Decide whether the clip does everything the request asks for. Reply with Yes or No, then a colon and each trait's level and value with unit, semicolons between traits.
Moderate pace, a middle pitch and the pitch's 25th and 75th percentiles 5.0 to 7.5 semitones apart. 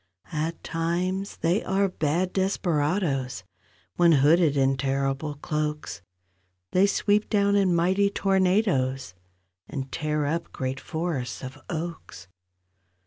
No: slow, 110 wpm; medium, 160 Hz; average, 5.3 semitones